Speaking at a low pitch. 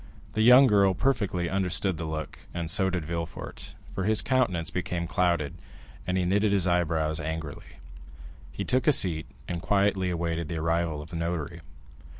Yes: very low, 85 Hz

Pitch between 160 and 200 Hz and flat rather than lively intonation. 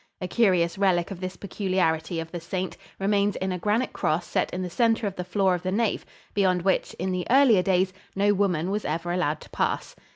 Yes: medium, 185 Hz; narrow, 2.3 semitones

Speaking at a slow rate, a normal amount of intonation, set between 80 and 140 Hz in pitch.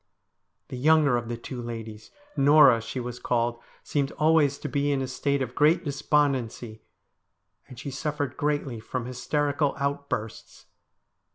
No: average, 145 wpm; average, 3.3 semitones; low, 135 Hz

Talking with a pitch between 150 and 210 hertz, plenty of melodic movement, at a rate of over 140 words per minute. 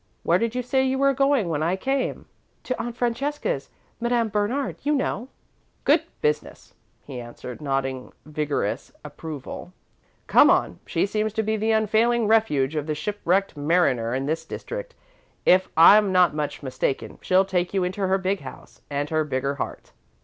Yes: high, 190 Hz; wide, 7.6 semitones; average, 165 wpm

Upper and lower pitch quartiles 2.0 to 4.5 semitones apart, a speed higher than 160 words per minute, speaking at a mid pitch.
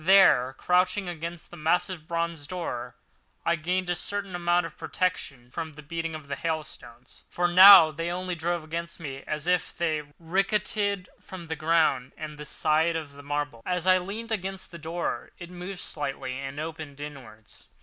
Yes: average, 3.3 semitones; average, 170 wpm; medium, 165 Hz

